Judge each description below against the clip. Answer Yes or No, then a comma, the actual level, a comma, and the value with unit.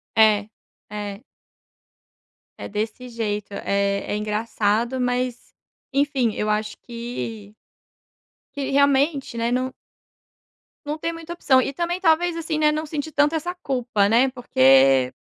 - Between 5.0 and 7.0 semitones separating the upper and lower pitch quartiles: Yes, wide, 5.6 semitones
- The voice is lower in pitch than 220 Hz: No, high, 245 Hz